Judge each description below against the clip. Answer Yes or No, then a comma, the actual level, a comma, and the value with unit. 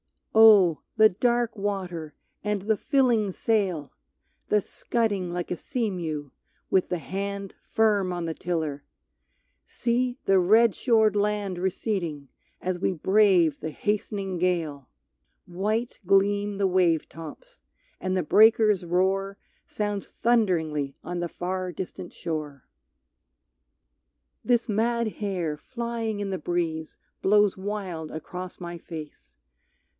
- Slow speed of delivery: Yes, slow, 120 wpm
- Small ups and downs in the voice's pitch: No, average, 3.6 semitones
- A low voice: No, high, 190 Hz